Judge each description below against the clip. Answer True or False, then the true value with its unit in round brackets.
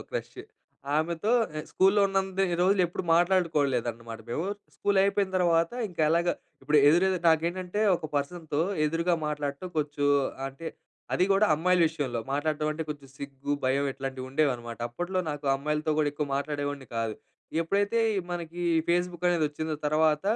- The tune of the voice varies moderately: True (3.7 semitones)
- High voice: False (155 Hz)